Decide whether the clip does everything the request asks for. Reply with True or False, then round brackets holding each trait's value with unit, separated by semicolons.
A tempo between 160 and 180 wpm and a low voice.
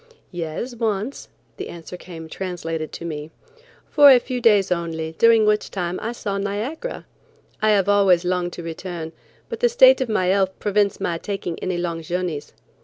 False (175 wpm; 185 Hz)